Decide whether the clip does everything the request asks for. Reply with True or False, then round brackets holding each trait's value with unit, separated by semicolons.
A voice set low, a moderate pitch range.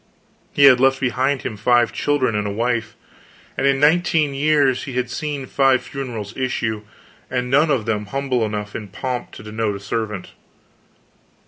True (125 Hz; 3.8 semitones)